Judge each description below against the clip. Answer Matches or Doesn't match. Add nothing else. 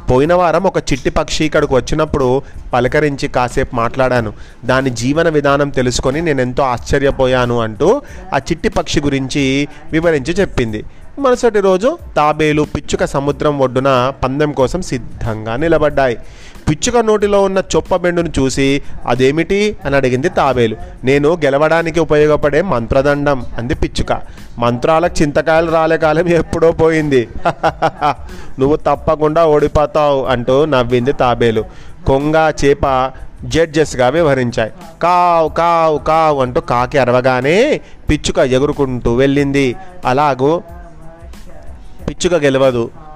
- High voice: Doesn't match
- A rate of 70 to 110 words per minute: Matches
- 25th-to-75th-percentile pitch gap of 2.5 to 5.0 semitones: Matches